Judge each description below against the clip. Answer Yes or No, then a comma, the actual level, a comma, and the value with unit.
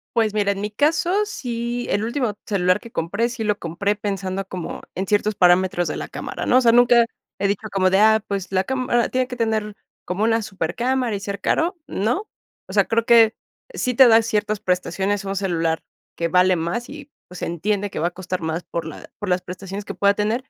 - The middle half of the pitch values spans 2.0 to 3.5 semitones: No, average, 4.0 semitones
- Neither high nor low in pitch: No, high, 205 Hz